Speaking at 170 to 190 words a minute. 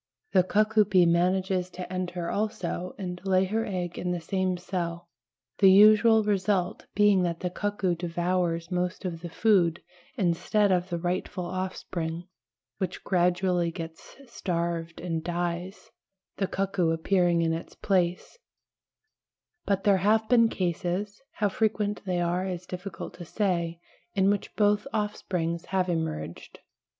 No: average, 140 wpm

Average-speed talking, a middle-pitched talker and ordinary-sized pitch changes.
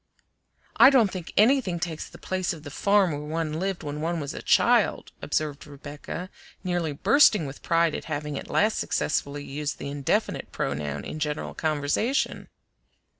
Yes: average, 165 wpm; medium, 155 Hz; average, 4.1 semitones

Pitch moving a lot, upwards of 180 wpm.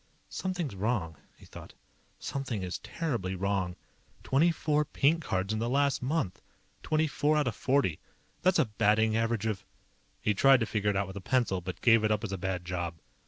Yes: wide, 6.3 semitones; average, 195 wpm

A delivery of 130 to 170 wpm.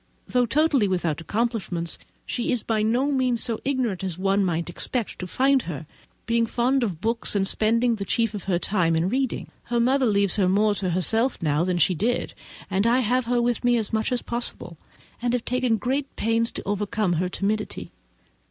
No: average, 195 wpm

